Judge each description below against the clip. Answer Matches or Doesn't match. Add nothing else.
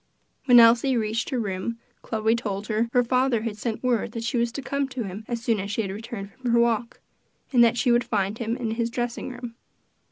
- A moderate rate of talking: Doesn't match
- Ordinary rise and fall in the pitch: Doesn't match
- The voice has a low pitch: Doesn't match